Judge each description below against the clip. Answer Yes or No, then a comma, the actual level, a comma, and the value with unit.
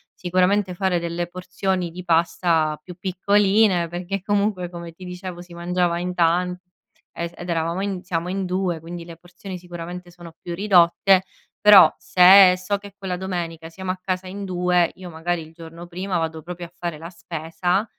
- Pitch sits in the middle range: Yes, medium, 180 Hz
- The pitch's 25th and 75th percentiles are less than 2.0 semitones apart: Yes, narrow, 1.6 semitones